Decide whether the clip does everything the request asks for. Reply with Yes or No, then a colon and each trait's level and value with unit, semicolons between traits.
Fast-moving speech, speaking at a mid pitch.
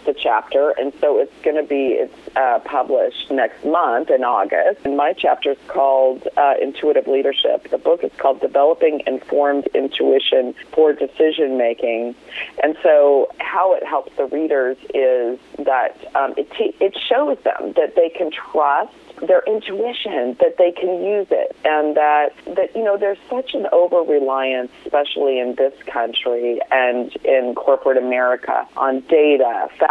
No: average, 160 wpm; medium, 150 Hz